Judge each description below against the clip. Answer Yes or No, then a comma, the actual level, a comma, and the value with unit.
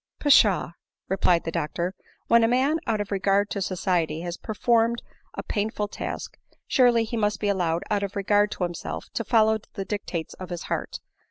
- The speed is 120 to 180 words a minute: No, average, 195 wpm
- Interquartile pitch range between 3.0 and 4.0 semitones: Yes, average, 3.7 semitones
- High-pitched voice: Yes, high, 205 Hz